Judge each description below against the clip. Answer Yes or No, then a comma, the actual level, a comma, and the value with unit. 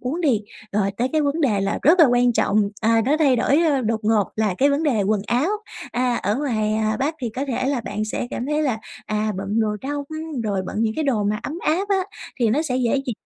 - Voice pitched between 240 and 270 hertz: Yes, high, 245 Hz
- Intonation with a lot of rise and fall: No, average, 4.9 semitones